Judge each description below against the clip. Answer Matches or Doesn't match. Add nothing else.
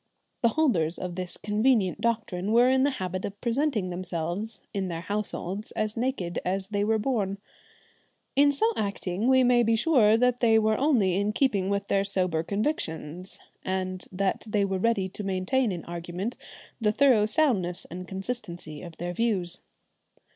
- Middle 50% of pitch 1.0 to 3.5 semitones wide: Doesn't match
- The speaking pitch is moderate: Doesn't match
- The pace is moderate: Matches